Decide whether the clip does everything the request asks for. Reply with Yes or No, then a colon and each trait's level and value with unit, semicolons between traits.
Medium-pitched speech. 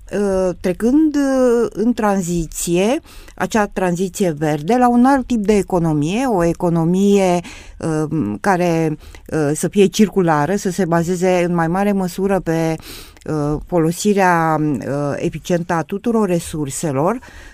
Yes: medium, 180 Hz